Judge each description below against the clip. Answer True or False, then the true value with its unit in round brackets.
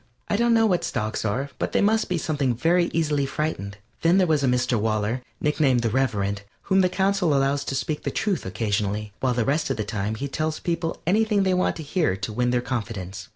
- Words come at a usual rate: False (225 wpm)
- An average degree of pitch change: False (7.5 semitones)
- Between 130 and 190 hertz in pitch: True (140 Hz)